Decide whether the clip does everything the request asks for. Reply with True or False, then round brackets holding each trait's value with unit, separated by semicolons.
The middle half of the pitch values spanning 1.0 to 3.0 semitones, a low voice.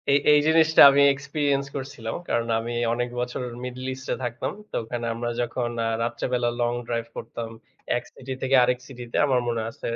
True (2.4 semitones; 125 Hz)